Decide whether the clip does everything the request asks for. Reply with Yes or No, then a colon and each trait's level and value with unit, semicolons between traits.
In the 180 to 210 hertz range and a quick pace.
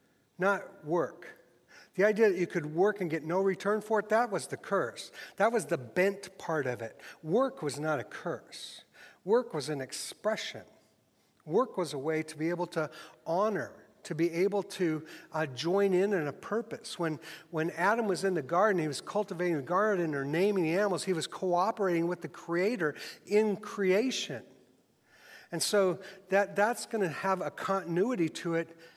No: medium, 185 Hz; average, 180 wpm